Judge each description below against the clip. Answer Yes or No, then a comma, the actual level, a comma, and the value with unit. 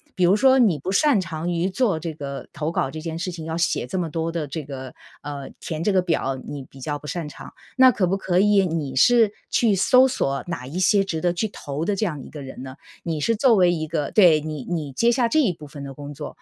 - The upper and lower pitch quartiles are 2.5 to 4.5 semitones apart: No, average, 4.9 semitones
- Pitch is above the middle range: No, medium, 165 Hz